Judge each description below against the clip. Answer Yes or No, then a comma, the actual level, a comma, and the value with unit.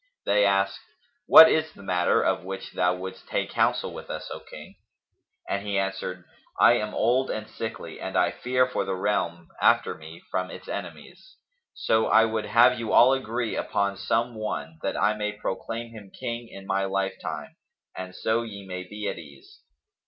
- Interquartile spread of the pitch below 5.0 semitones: Yes, average, 3.3 semitones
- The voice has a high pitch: No, low, 100 Hz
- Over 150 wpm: Yes, average, 180 wpm